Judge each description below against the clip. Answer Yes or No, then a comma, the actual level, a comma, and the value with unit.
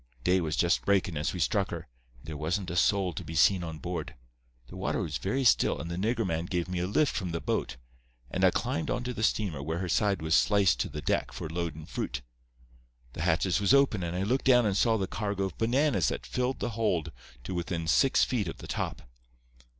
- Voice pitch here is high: No, very low, 90 Hz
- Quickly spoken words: Yes, fast, 230 wpm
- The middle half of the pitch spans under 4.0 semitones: No, average, 4.6 semitones